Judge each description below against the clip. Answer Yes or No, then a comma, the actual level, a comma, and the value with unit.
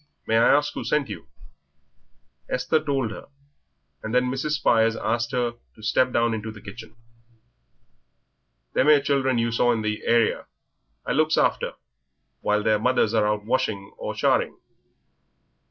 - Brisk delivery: No, average, 155 wpm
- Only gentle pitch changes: No, average, 3.1 semitones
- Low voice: Yes, low, 115 Hz